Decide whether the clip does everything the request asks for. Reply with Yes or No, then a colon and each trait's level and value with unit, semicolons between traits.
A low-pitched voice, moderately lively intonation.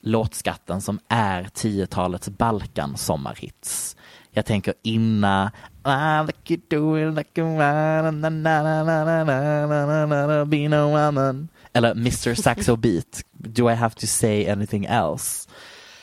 No: low, 120 Hz; wide, 5.9 semitones